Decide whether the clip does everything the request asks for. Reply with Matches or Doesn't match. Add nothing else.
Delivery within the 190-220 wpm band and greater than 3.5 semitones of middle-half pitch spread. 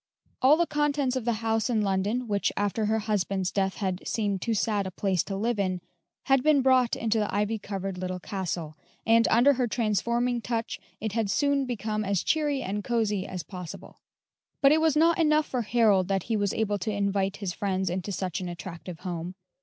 Matches